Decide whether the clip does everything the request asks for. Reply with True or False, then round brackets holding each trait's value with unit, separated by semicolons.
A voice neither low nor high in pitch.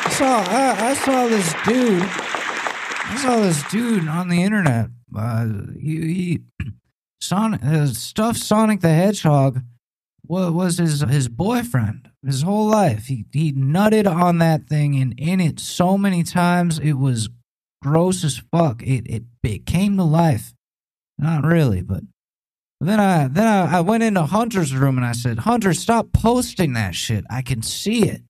True (165 Hz)